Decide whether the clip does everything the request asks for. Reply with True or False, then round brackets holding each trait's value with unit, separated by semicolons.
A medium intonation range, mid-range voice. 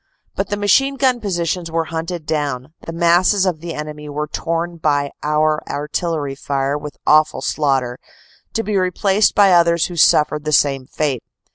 True (3.0 semitones; 160 Hz)